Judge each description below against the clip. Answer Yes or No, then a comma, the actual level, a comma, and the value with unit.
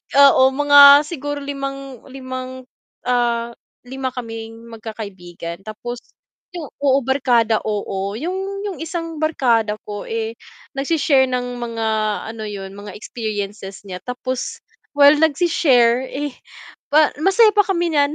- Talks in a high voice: Yes, very high, 255 Hz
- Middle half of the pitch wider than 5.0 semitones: No, average, 4.4 semitones